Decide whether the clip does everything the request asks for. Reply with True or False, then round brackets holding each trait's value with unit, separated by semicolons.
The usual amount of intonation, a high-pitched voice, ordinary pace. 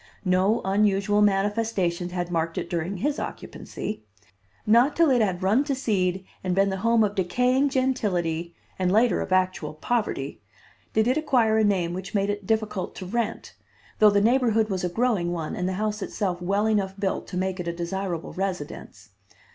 True (3.5 semitones; 195 Hz; 180 wpm)